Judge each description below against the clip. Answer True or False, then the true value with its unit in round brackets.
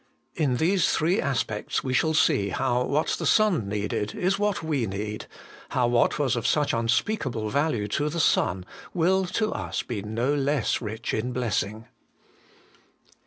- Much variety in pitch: True (6.3 semitones)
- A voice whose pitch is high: False (130 Hz)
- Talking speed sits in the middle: True (160 wpm)